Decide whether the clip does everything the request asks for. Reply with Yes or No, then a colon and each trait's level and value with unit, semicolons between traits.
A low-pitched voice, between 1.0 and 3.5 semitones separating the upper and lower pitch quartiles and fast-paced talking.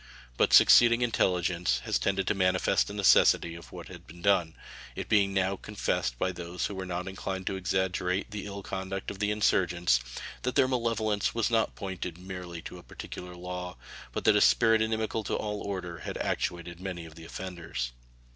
No: very low, 95 Hz; average, 2.7 semitones; average, 185 wpm